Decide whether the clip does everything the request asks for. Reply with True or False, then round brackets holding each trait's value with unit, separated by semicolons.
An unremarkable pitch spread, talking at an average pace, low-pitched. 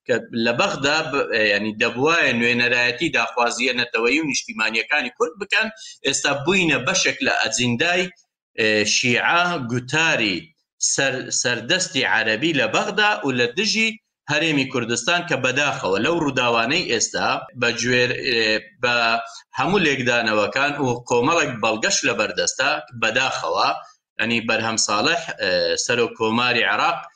False (7.2 semitones; 105 wpm; 130 Hz)